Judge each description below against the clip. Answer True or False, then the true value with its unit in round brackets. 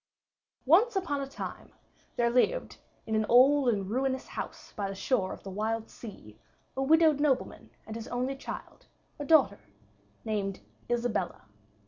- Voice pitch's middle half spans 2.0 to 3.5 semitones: False (4.4 semitones)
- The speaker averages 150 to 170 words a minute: True (155 wpm)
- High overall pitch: True (245 Hz)